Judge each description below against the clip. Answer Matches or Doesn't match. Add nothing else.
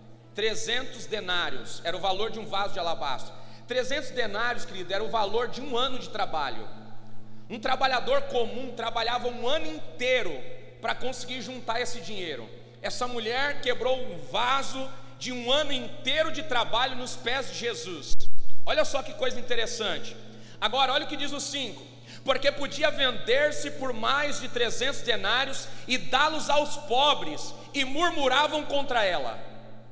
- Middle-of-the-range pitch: Doesn't match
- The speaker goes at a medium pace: Matches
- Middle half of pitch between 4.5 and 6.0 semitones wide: Doesn't match